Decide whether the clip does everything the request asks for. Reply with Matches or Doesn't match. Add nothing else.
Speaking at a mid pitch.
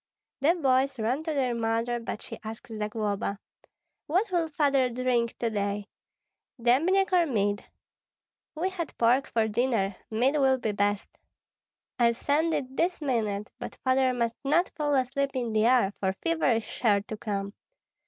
Doesn't match